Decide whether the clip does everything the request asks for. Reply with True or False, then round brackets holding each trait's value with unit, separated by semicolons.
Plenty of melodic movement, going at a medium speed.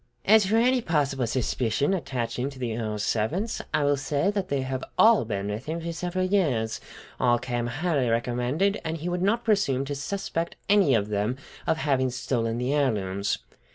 True (6.9 semitones; 185 wpm)